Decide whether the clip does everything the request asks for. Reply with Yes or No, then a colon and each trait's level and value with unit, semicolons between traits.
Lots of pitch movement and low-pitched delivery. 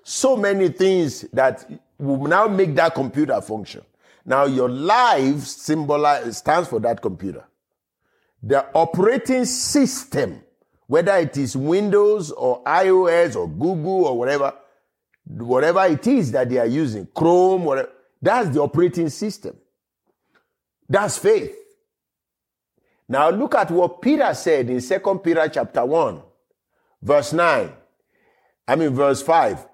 No: wide, 6.1 semitones; medium, 170 Hz